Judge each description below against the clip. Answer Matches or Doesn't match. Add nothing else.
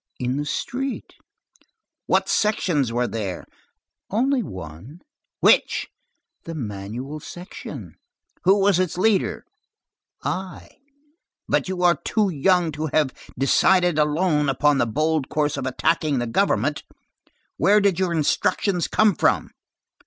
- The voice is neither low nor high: Matches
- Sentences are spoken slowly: Matches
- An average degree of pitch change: Doesn't match